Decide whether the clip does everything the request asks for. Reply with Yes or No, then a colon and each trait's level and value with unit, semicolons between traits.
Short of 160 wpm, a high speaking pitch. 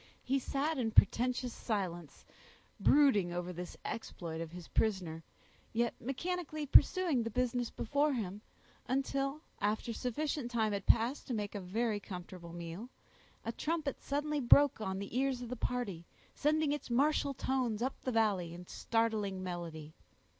Yes: average, 150 wpm; high, 230 Hz